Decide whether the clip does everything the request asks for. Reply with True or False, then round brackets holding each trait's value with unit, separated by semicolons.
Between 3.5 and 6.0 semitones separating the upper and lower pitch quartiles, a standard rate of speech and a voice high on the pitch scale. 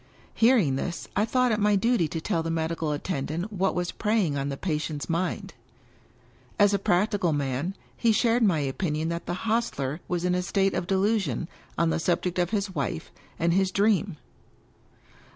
False (4.2 semitones; 180 wpm; 180 Hz)